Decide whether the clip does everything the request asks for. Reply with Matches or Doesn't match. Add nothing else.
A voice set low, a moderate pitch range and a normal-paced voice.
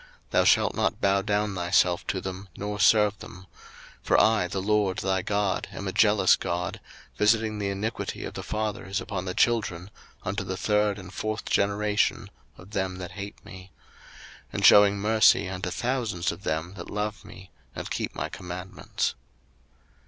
Doesn't match